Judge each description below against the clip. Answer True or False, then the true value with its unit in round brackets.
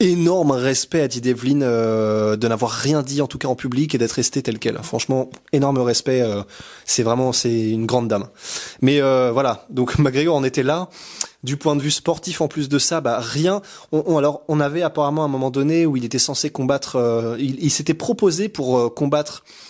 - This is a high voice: False (140 Hz)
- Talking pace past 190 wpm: True (220 wpm)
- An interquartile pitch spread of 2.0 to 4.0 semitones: True (3.3 semitones)